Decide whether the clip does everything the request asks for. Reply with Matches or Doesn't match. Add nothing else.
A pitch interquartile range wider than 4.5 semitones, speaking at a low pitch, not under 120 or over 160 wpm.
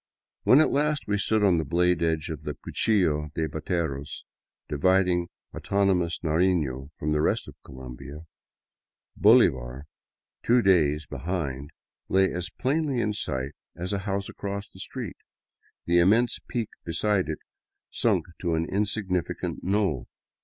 Matches